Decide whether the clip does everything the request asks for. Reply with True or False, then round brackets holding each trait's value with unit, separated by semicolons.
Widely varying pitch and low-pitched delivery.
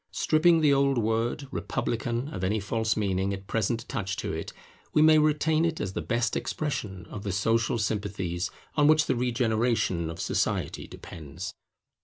True (6.0 semitones; 115 Hz)